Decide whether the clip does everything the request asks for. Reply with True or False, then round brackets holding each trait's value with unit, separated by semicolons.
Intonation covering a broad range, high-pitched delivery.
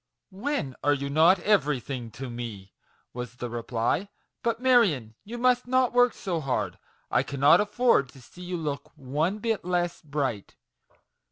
False (8.3 semitones; 155 Hz)